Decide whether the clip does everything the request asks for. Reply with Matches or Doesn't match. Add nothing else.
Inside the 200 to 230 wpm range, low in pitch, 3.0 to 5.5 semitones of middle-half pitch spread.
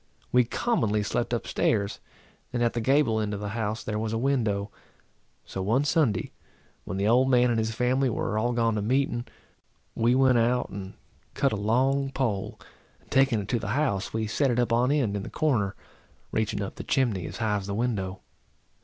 Matches